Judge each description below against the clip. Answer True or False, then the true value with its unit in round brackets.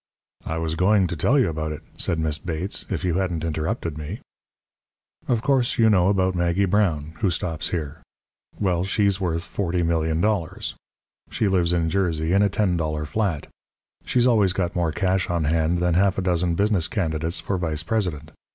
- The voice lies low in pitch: True (90 Hz)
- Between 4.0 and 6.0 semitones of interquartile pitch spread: False (3.3 semitones)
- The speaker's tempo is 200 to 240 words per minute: False (180 wpm)